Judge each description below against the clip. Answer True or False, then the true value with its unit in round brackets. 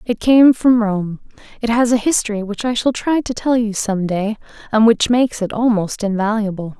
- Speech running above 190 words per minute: True (205 wpm)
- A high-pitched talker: True (220 Hz)